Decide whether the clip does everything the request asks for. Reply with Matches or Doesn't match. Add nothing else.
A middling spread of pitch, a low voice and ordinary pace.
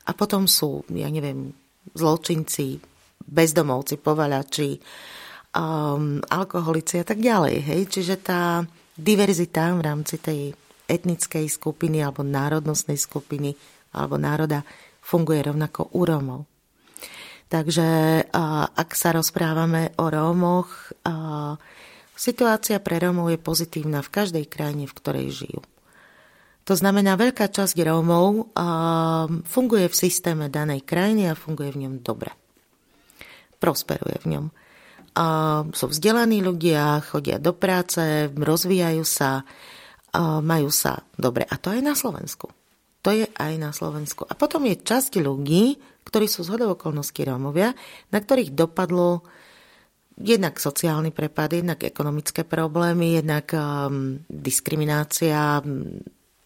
Doesn't match